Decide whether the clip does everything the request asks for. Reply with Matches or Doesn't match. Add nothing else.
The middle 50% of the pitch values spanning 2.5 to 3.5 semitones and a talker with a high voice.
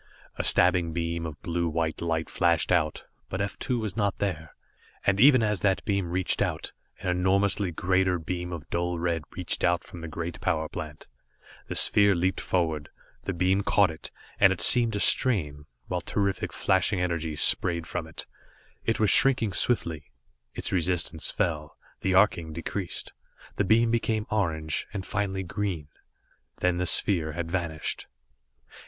Doesn't match